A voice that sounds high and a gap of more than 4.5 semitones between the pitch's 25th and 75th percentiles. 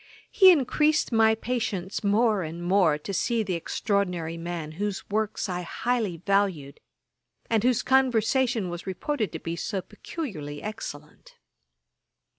Yes: high, 200 Hz; average, 5.0 semitones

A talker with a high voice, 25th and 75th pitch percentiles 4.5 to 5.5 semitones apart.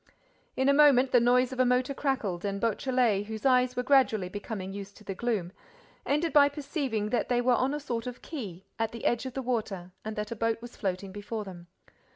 No: high, 235 Hz; average, 3.9 semitones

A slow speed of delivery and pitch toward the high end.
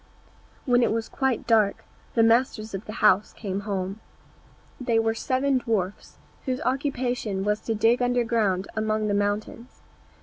No: average, 145 wpm; high, 225 Hz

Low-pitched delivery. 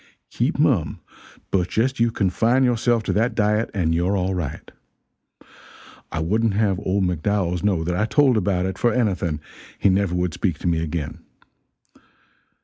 Yes: very low, 95 Hz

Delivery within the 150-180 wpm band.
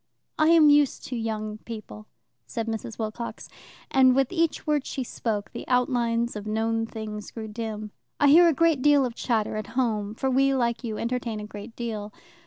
No: average, 190 wpm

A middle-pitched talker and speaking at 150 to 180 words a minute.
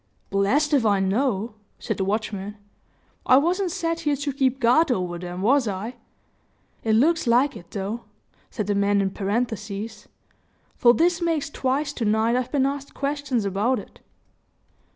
No: high, 235 Hz; average, 160 wpm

